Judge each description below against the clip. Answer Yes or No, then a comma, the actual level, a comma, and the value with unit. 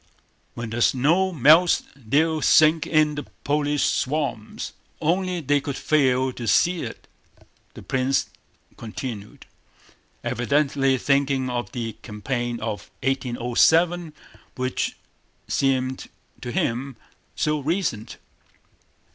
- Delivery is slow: Yes, slow, 105 wpm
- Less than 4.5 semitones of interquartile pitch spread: Yes, average, 3.9 semitones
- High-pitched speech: No, low, 135 Hz